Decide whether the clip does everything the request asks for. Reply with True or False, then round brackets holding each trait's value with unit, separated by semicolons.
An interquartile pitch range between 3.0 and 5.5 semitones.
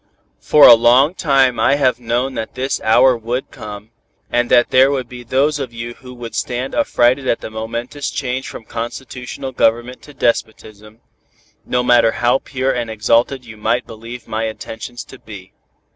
False (2.4 semitones)